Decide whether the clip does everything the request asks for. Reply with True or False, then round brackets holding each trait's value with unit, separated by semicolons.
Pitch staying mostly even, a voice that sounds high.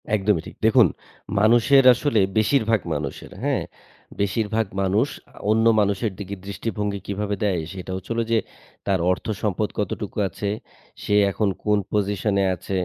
False (2.1 semitones; 105 Hz)